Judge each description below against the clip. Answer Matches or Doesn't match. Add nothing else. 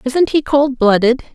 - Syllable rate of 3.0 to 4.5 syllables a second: Matches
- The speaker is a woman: Matches